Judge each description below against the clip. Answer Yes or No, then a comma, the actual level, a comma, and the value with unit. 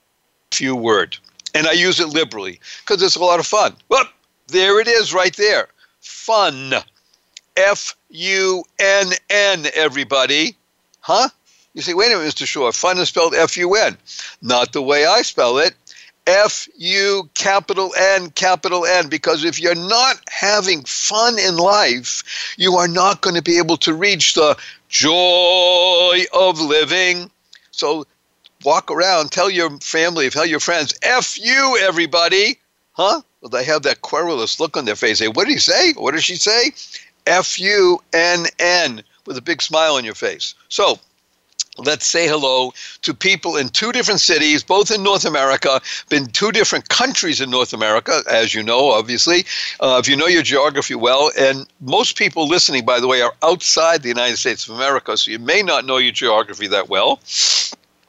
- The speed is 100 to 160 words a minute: No, average, 175 wpm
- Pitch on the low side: No, medium, 175 Hz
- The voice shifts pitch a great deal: No, average, 4.5 semitones